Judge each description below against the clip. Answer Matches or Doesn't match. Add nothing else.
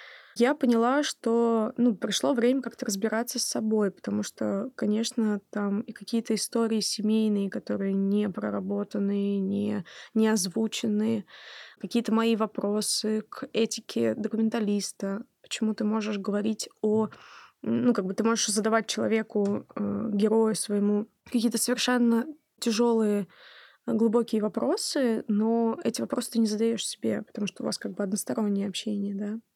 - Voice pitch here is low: Doesn't match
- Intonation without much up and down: Matches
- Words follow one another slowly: Doesn't match